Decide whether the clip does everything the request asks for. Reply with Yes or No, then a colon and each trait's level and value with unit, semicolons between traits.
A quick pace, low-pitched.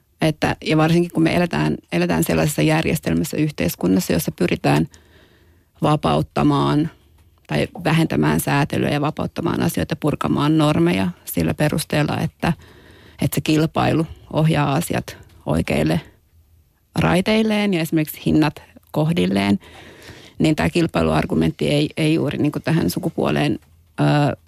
No: average, 115 wpm; low, 100 Hz